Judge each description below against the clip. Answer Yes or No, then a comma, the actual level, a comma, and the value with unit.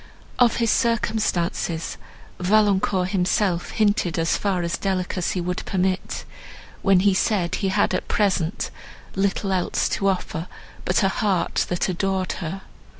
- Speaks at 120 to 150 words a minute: Yes, slow, 135 wpm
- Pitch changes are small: Yes, narrow, 2.1 semitones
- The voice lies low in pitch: No, high, 190 Hz